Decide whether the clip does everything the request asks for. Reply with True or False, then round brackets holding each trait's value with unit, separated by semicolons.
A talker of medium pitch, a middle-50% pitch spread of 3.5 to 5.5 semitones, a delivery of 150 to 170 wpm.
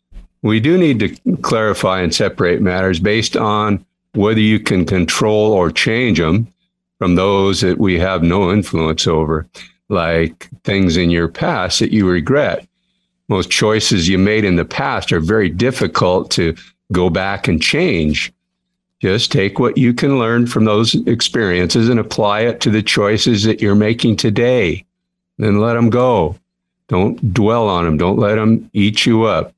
False (105 Hz; 4.2 semitones; 165 wpm)